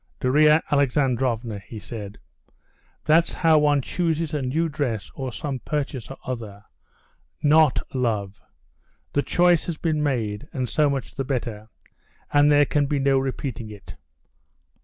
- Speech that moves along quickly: No, average, 140 wpm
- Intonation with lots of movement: No, average, 4.2 semitones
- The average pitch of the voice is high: No, low, 135 Hz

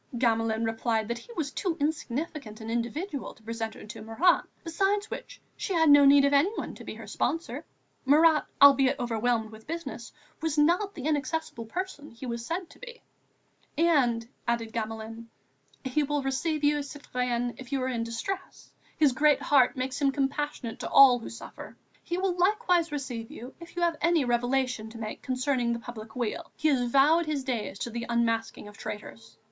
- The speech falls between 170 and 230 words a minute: Yes, average, 185 wpm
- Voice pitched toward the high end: Yes, very high, 265 Hz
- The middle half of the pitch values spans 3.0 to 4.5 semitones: No, average, 5.2 semitones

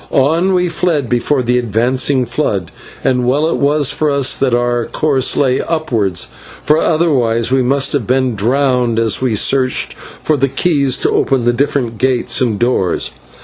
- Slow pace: No, average, 170 wpm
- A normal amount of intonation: Yes, average, 3.0 semitones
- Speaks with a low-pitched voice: Yes, low, 130 Hz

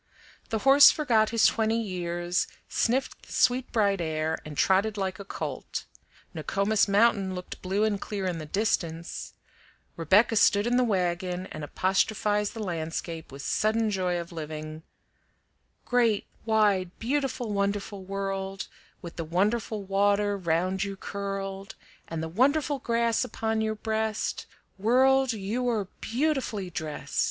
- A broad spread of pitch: No, average, 3.5 semitones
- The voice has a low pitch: No, high, 200 Hz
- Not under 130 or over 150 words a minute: Yes, average, 140 wpm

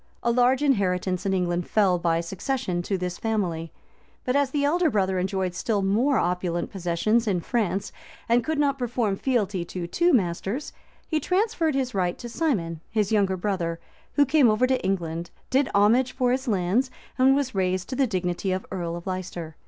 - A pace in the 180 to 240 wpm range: Yes, average, 185 wpm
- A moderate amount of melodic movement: No, wide, 6.2 semitones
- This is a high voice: Yes, high, 200 Hz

